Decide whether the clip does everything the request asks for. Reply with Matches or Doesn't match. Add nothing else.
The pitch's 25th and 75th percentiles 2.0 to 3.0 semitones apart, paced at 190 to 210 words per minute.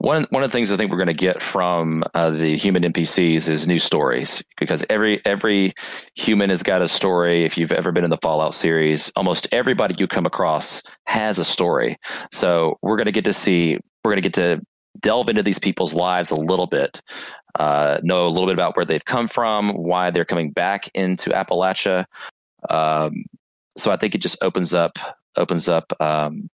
Matches